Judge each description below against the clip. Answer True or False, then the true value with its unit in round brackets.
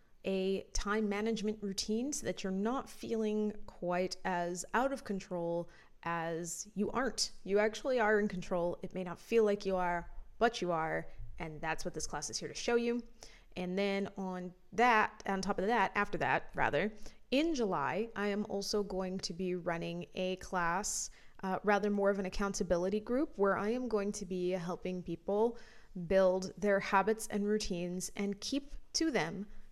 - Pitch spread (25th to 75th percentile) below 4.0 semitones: True (2.8 semitones)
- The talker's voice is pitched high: True (195 Hz)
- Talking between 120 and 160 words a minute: False (180 wpm)